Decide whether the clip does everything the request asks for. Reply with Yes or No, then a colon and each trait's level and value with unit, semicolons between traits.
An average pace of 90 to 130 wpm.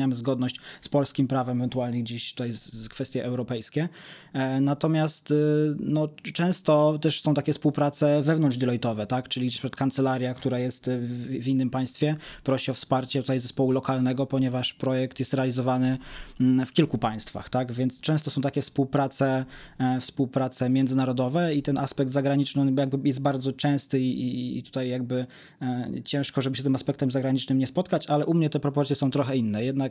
No: average, 155 wpm